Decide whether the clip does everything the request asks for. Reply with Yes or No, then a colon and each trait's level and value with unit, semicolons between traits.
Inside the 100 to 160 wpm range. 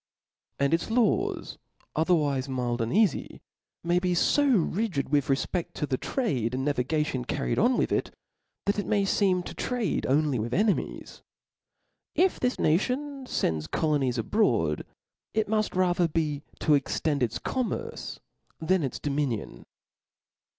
Yes: average, 140 wpm